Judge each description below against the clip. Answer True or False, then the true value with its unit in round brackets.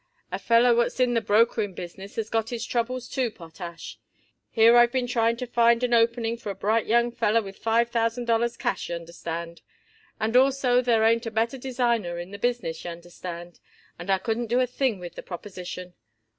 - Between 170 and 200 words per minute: True (190 wpm)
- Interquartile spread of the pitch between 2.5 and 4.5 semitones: True (3.8 semitones)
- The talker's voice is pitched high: True (230 Hz)